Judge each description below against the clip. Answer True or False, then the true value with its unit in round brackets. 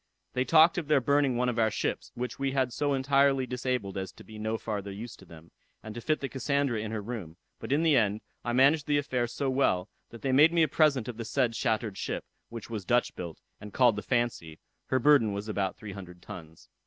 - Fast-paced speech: True (235 wpm)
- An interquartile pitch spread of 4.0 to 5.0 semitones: True (4.6 semitones)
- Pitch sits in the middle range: False (120 Hz)